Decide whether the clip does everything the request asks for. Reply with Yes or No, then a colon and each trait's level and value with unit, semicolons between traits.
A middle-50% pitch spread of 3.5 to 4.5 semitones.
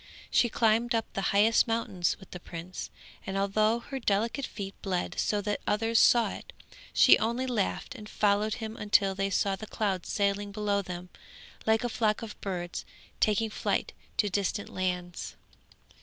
No: narrow, 2.4 semitones